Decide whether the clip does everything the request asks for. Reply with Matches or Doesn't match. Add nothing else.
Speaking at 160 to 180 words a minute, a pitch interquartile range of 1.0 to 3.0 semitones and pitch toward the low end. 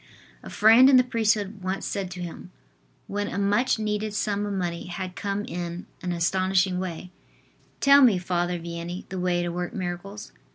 Doesn't match